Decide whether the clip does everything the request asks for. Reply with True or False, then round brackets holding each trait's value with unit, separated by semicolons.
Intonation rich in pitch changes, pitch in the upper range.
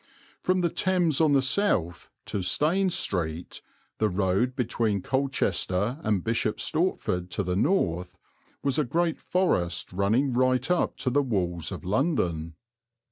False (8.5 semitones; 115 Hz)